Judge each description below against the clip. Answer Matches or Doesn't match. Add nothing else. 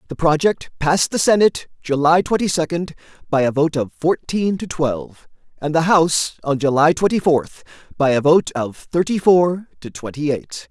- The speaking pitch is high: Doesn't match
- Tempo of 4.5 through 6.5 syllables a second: Matches